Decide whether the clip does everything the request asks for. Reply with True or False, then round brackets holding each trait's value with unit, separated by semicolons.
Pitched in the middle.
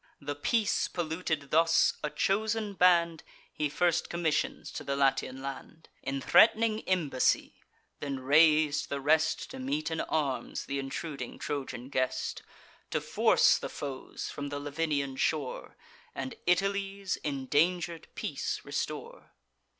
True (155 Hz)